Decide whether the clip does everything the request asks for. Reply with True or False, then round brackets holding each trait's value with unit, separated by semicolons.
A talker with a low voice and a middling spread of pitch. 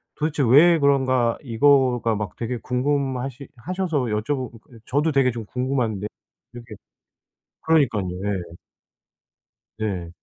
True (125 Hz; 4.1 semitones)